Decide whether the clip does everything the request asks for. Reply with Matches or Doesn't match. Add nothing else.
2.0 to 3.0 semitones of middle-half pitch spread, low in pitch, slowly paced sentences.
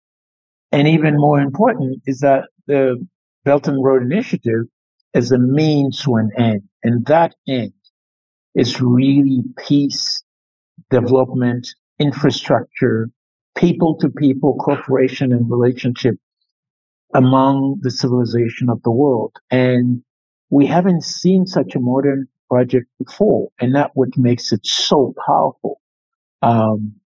Matches